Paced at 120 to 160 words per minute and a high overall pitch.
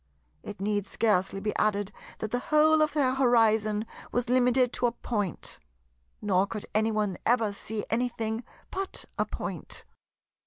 Yes: average, 150 wpm; high, 220 Hz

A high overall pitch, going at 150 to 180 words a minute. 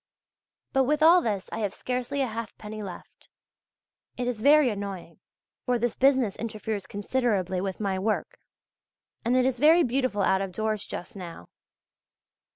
Yes: high, 220 Hz; average, 155 wpm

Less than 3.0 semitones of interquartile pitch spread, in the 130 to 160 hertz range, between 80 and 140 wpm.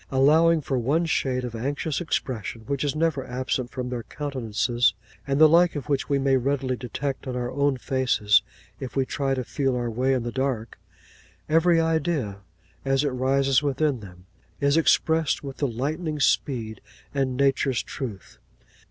No: narrow, 2.6 semitones; low, 135 Hz; average, 170 wpm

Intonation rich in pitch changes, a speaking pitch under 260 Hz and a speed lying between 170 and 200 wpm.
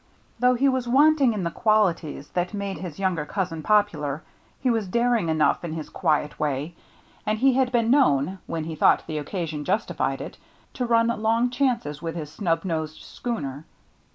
Yes: wide, 7.0 semitones; high, 190 Hz; average, 180 wpm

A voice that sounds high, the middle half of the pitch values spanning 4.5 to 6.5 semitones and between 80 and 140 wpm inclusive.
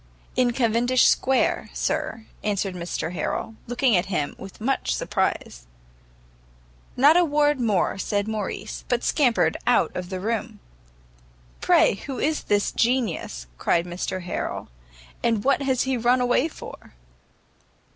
Yes: high, 230 Hz; average, 5.3 semitones; slow, 135 wpm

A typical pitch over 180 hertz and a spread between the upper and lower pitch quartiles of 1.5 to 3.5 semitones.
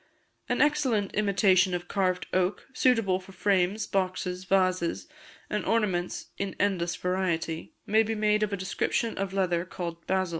Yes: high, 190 Hz; narrow, 2.5 semitones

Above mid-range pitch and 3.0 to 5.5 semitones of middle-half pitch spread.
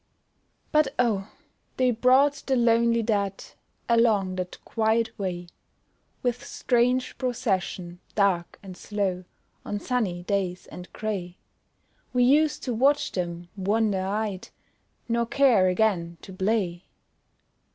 Yes: high, 215 Hz; average, 4.7 semitones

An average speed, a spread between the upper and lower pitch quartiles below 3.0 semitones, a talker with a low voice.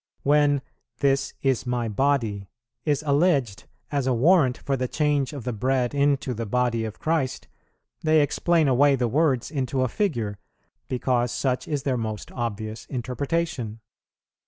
No: average, 150 wpm; average, 3.3 semitones; low, 130 Hz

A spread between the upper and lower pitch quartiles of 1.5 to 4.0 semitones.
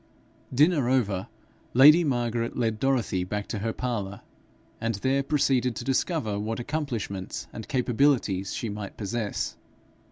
No: average, 4.4 semitones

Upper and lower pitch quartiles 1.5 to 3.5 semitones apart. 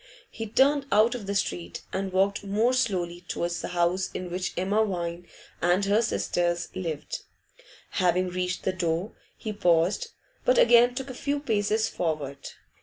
No: average, 4.1 semitones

